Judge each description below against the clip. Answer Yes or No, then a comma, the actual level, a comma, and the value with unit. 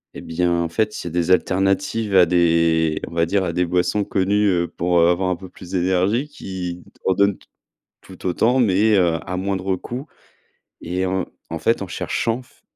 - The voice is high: No, very low, 95 Hz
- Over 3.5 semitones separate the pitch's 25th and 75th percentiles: No, narrow, 2.4 semitones